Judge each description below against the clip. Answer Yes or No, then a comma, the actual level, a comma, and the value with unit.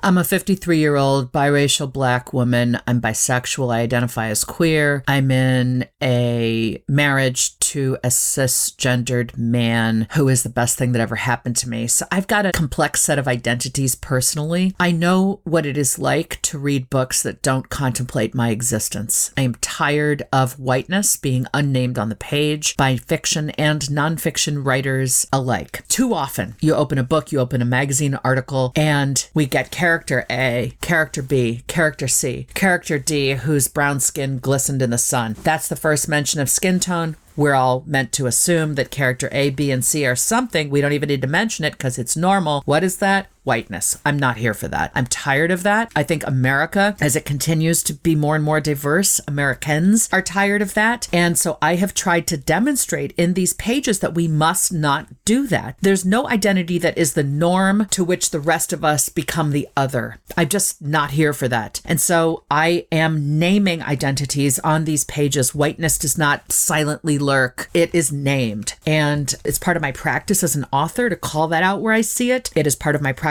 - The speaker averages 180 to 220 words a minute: Yes, average, 195 wpm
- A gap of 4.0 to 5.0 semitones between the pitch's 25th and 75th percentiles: Yes, average, 4.4 semitones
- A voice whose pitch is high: No, medium, 145 Hz